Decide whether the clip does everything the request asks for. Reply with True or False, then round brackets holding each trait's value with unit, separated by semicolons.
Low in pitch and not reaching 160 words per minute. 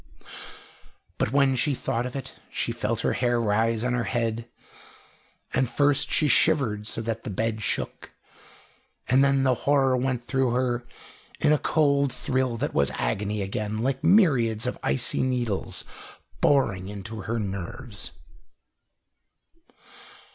True (120 Hz; 140 wpm)